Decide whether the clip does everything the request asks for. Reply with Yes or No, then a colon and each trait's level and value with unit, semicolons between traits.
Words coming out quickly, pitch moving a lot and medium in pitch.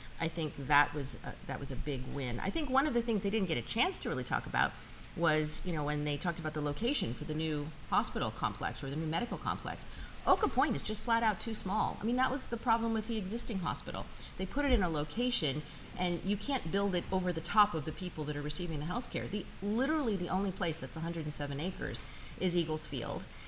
Yes: fast, 245 wpm; wide, 6.3 semitones; medium, 175 Hz